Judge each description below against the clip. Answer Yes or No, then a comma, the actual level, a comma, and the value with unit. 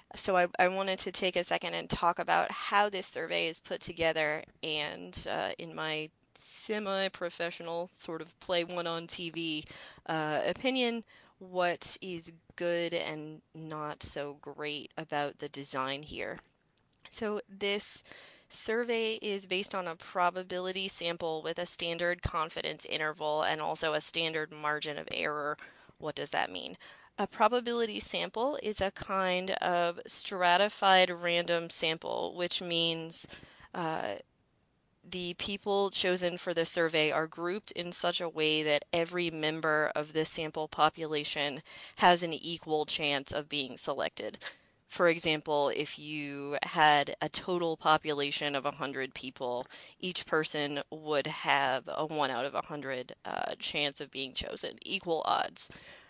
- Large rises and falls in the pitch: No, average, 3.1 semitones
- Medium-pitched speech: Yes, medium, 165 Hz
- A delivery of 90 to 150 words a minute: Yes, average, 140 wpm